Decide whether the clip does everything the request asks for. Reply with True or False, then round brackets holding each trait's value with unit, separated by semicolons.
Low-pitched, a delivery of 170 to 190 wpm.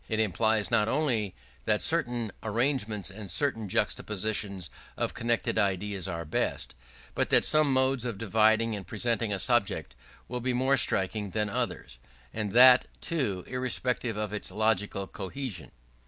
False (110 Hz; 145 wpm)